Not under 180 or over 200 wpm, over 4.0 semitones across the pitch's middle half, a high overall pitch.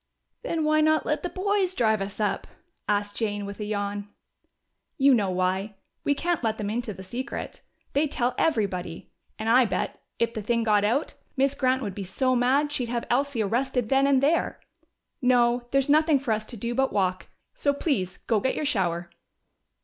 Yes: average, 190 wpm; average, 5.1 semitones; high, 240 Hz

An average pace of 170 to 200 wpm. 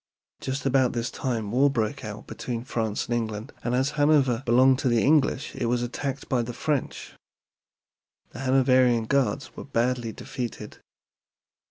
No: average, 155 wpm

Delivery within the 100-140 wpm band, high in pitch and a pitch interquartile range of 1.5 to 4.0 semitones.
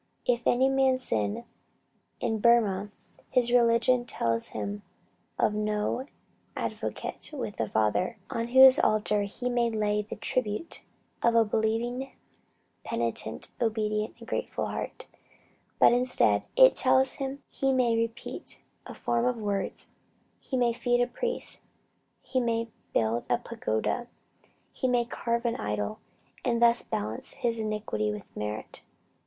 Yes: slow, 135 wpm; high, 230 Hz; average, 3.0 semitones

